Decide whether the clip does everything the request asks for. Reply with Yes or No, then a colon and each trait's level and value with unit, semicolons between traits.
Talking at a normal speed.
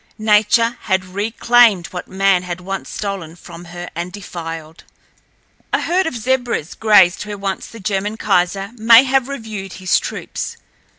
Yes: average, 145 wpm